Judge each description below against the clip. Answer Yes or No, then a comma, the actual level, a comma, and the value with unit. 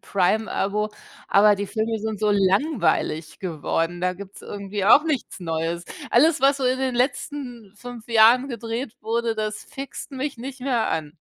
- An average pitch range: Yes, average, 4.4 semitones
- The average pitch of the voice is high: Yes, high, 220 Hz